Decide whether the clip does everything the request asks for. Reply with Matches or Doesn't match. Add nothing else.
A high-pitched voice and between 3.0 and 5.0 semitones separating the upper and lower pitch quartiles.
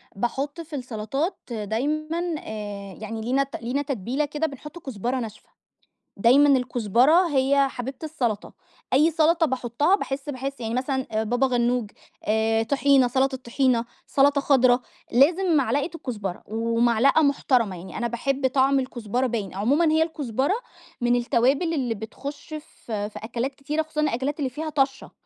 Matches